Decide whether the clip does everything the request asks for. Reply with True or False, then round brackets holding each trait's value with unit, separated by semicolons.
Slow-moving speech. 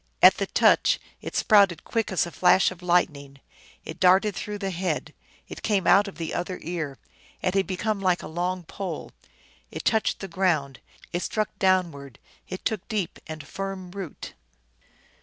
False (170 wpm)